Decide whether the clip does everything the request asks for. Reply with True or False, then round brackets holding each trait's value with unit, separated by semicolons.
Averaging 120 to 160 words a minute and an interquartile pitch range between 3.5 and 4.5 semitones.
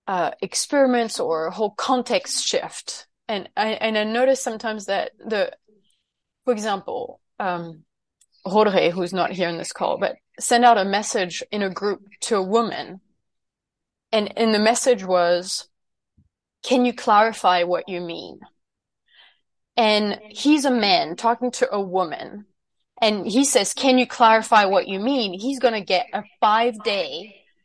True (150 wpm; 4.1 semitones)